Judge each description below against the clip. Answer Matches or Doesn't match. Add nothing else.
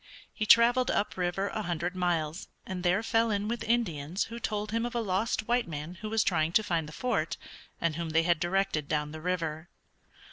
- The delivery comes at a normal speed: Doesn't match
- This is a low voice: Doesn't match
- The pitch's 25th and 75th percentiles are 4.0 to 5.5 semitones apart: Matches